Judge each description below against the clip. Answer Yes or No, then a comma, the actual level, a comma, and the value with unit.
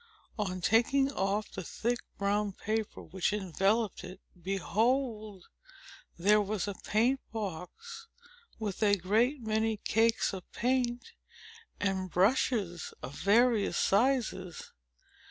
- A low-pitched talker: No, high, 210 Hz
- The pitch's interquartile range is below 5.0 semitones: Yes, average, 3.5 semitones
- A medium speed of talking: No, slow, 110 wpm